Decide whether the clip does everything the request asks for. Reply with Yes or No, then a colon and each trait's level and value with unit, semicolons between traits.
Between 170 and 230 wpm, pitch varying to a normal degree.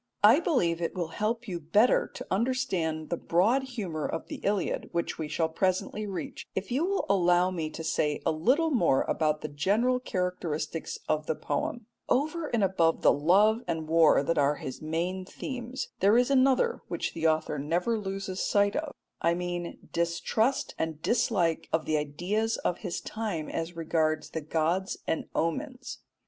No: average, 175 wpm; wide, 5.7 semitones